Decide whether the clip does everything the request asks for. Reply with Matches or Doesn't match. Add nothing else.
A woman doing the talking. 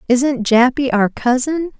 Matches